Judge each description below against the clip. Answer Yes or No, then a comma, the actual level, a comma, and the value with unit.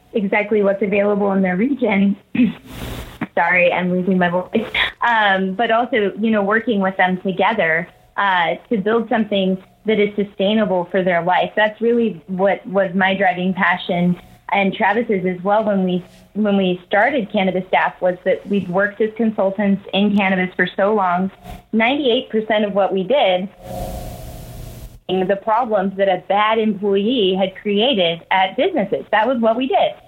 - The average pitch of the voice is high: Yes, high, 200 Hz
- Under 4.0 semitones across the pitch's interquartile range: Yes, narrow, 2.5 semitones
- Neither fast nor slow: Yes, average, 160 wpm